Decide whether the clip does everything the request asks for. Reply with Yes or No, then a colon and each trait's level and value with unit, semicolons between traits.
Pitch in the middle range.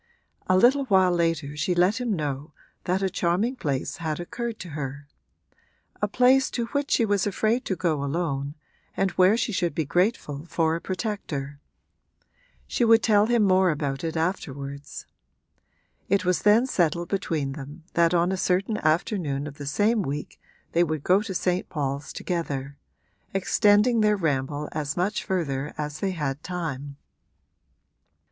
Yes: medium, 175 Hz